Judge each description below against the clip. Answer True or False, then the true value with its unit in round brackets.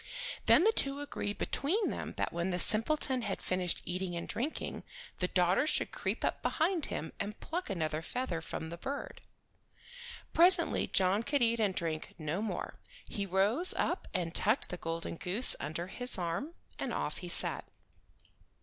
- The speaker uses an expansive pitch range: True (8.0 semitones)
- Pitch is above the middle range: True (200 Hz)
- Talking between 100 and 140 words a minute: False (170 wpm)